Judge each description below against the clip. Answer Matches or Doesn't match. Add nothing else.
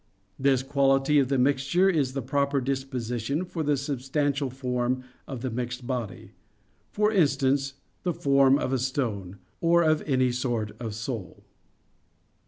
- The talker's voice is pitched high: Doesn't match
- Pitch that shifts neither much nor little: Doesn't match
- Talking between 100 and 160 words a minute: Matches